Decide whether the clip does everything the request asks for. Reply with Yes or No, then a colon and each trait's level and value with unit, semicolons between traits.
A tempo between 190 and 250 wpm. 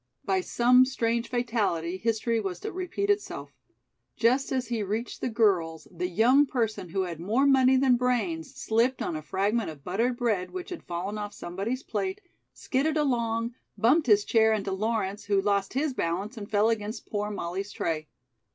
No: average, 175 wpm